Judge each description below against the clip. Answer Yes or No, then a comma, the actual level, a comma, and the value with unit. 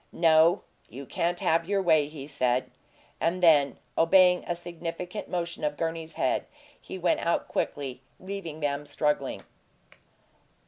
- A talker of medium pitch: Yes, medium, 165 Hz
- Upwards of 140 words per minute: No, slow, 135 wpm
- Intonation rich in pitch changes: No, average, 3.1 semitones